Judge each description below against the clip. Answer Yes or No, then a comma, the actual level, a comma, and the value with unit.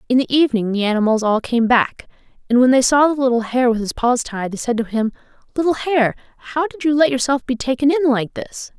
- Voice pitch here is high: Yes, very high, 250 Hz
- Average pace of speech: No, fast, 240 wpm